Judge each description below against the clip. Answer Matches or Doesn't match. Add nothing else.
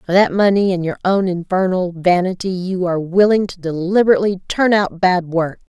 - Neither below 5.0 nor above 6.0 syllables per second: Matches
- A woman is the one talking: Matches